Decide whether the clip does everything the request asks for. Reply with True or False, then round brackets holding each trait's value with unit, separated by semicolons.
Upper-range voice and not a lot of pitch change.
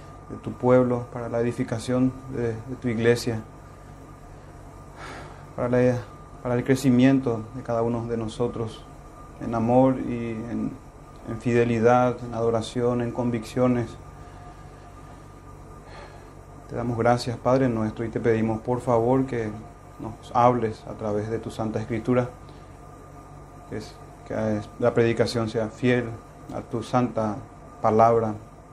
False (120 Hz; 1.7 semitones)